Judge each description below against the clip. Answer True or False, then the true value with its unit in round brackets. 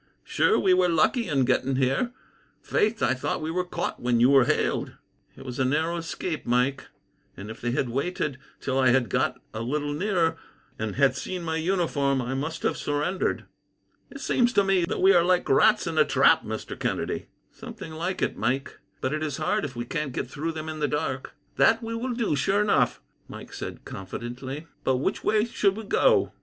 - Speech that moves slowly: False (205 wpm)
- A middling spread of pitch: False (5.8 semitones)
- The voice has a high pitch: False (150 Hz)